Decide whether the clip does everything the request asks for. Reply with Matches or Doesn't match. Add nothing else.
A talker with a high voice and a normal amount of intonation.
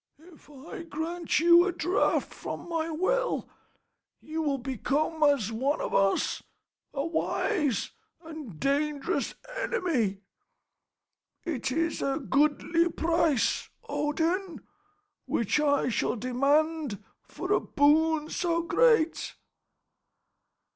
Matches